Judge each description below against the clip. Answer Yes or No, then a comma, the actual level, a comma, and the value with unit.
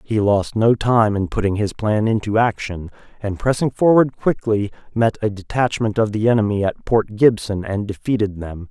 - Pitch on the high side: No, low, 110 Hz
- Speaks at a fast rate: No, average, 180 wpm